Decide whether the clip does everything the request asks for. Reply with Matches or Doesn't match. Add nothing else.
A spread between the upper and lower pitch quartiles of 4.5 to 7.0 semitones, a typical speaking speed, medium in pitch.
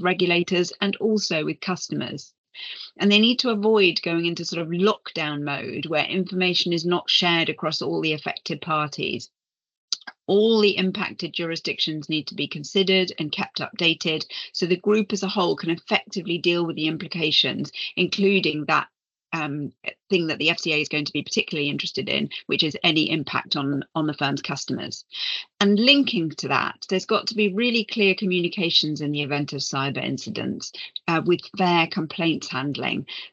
Doesn't match